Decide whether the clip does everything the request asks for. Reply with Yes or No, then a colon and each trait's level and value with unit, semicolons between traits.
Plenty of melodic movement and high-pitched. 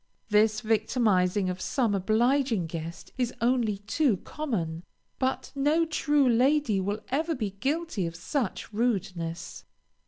Yes: wide, 6.0 semitones; high, 220 Hz